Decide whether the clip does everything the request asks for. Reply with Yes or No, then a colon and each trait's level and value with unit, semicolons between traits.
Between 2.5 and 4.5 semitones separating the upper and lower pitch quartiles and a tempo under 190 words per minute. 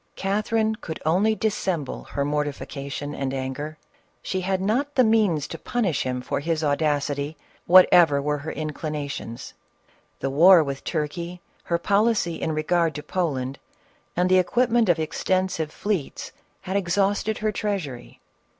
No: average, 5.0 semitones; average, 140 wpm